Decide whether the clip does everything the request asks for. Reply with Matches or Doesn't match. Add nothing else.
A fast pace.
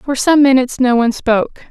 Matches